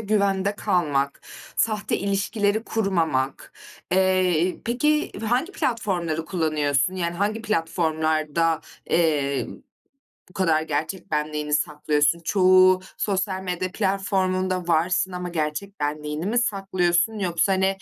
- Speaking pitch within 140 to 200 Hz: Yes, medium, 185 Hz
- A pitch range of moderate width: Yes, average, 3.9 semitones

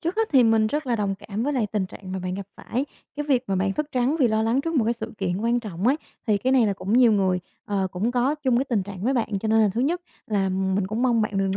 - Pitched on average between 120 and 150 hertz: No, high, 220 Hz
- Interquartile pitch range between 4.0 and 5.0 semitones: Yes, average, 4.4 semitones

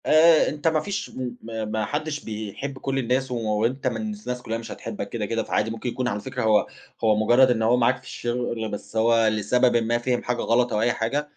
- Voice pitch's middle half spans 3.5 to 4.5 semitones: No, average, 2.7 semitones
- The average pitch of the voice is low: Yes, low, 120 Hz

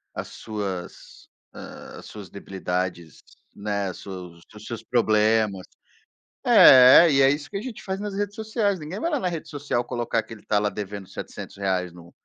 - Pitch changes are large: Yes, wide, 8.6 semitones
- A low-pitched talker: Yes, low, 115 Hz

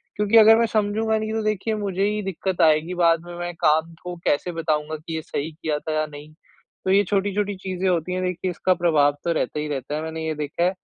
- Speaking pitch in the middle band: Yes, medium, 175 Hz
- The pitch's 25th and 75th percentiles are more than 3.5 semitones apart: Yes, average, 4.1 semitones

